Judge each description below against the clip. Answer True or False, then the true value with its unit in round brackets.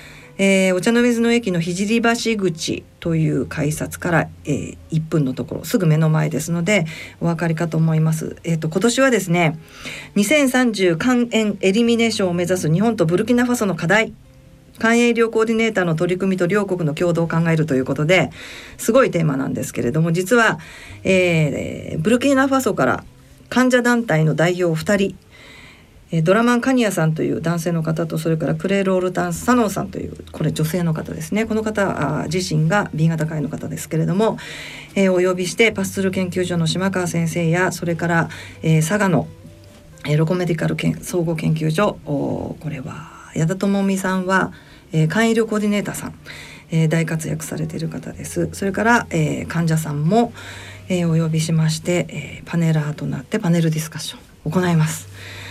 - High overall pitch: False (170 Hz)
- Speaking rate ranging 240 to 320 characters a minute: False (370 characters per minute)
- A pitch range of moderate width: True (4.3 semitones)